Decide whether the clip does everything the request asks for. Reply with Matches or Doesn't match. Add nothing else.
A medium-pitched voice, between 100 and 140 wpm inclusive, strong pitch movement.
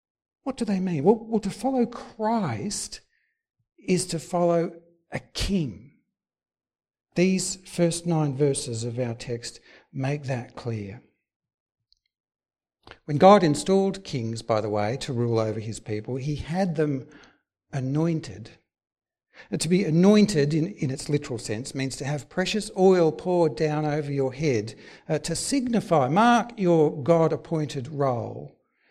Matches